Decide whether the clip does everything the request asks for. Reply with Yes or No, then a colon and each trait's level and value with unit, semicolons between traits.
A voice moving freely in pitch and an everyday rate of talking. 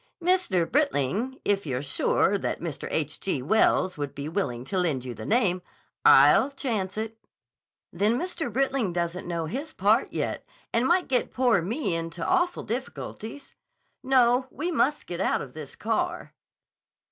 Yes: wide, 7.9 semitones; average, 155 wpm